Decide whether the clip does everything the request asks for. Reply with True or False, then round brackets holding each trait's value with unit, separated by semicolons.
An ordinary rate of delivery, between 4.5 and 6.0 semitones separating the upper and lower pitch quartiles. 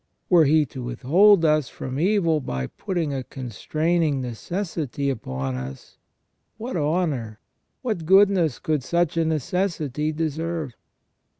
False (120 wpm; 4.8 semitones)